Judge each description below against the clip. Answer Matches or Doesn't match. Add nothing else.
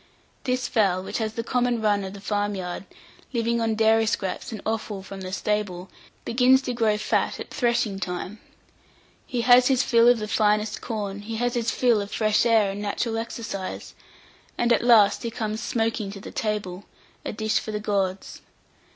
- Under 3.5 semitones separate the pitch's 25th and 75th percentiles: Matches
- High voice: Matches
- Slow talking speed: Doesn't match